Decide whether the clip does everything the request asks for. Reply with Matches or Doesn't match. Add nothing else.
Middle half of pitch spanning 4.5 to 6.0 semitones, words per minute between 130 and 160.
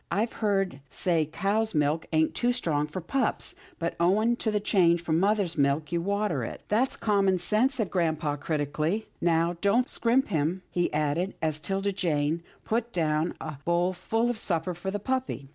Doesn't match